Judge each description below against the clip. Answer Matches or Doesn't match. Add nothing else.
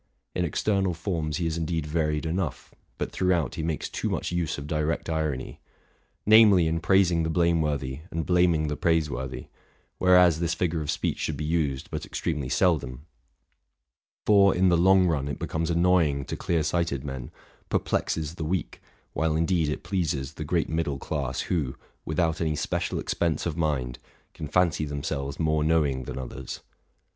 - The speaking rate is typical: Matches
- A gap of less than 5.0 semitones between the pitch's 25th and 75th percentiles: Matches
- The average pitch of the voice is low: Matches